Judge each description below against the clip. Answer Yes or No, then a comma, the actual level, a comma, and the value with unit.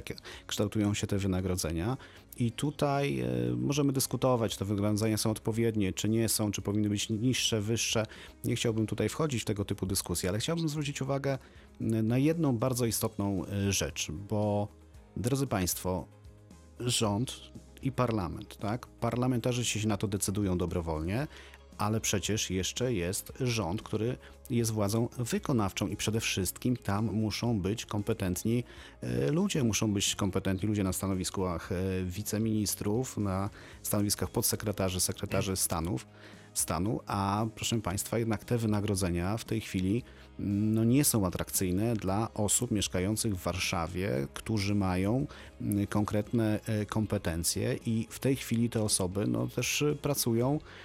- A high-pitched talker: No, low, 105 Hz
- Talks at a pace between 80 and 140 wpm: Yes, average, 130 wpm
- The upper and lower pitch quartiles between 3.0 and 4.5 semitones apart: Yes, average, 3.4 semitones